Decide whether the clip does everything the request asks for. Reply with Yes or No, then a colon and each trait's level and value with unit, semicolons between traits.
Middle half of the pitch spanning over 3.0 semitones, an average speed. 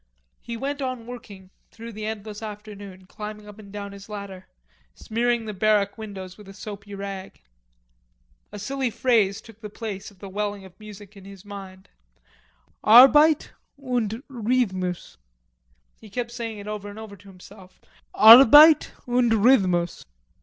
No: average, 2.7 semitones; average, 150 wpm